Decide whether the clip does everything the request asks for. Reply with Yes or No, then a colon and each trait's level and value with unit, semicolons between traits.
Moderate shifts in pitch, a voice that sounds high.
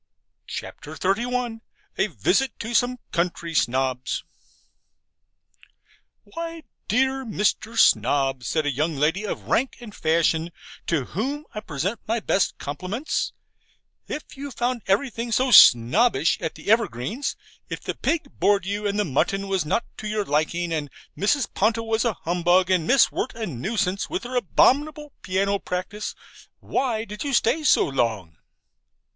No: wide, 6.7 semitones; high, 205 Hz